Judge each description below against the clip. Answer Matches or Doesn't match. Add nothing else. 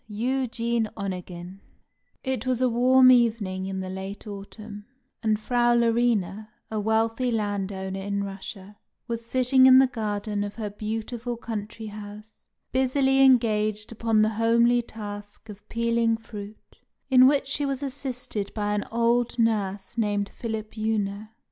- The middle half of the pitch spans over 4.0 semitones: Doesn't match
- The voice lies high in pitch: Matches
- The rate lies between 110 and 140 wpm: Matches